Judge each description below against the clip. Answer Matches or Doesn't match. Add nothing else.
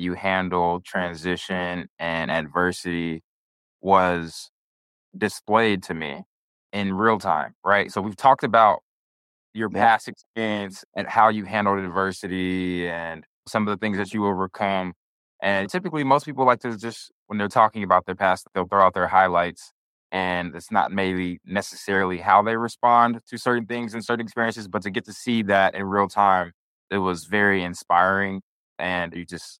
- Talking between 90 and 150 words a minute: Doesn't match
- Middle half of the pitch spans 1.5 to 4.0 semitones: Matches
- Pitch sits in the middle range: Doesn't match